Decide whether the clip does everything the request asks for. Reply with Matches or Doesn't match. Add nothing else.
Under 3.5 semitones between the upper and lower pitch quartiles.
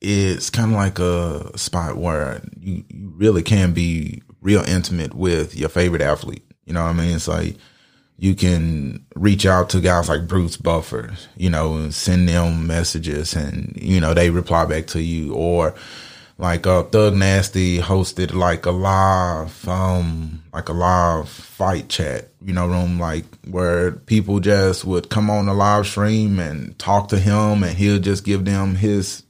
Matches